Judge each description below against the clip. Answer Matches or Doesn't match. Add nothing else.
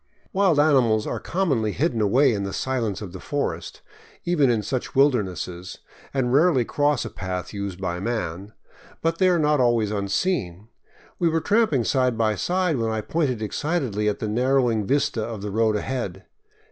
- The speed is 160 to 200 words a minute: Matches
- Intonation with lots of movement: Matches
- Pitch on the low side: Matches